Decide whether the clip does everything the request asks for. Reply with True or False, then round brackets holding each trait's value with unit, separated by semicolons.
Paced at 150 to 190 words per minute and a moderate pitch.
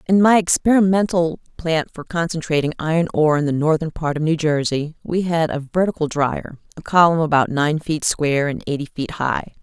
True (185 wpm; 160 Hz)